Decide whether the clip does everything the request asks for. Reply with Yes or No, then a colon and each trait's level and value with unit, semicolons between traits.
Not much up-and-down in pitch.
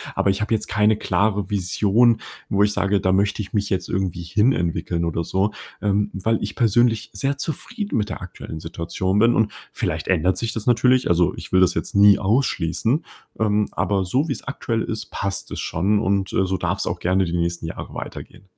No: average, 3.2 semitones